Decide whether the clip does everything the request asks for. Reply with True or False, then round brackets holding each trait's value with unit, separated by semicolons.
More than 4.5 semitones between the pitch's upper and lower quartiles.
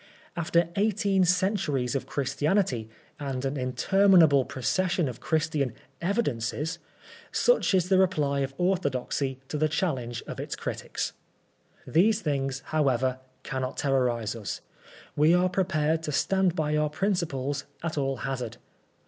True (5.2 semitones)